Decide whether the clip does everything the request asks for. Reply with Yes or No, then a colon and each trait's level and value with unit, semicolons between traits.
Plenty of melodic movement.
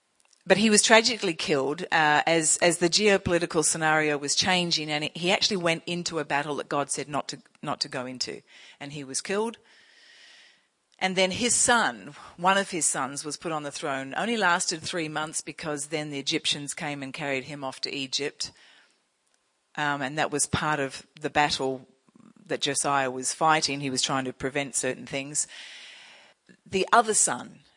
No: average, 3.7 semitones